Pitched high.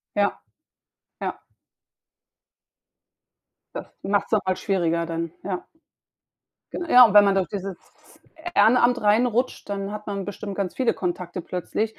Yes: high, 200 Hz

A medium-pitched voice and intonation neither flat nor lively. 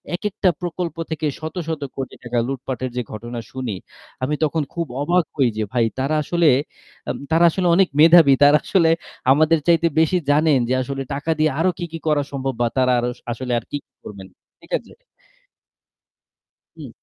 Yes: medium, 150 Hz; average, 4.2 semitones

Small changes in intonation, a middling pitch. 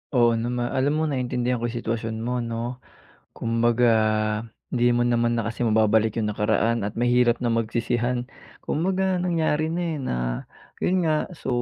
No: narrow, 1.9 semitones; low, 120 Hz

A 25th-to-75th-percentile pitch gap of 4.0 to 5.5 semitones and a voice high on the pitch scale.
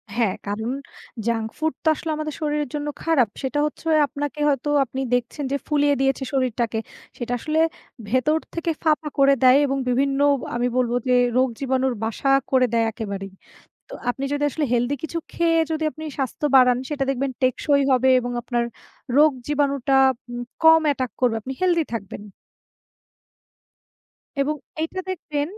No: average, 3.3 semitones; very high, 275 Hz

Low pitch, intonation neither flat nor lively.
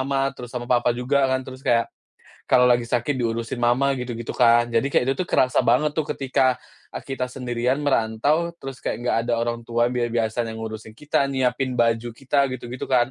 No: low, 125 Hz; narrow, 2.2 semitones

